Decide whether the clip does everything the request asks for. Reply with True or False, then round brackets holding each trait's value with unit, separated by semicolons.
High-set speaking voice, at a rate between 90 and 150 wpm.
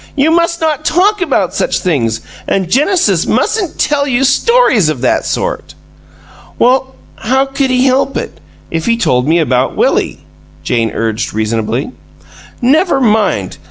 True (255 Hz; 145 wpm)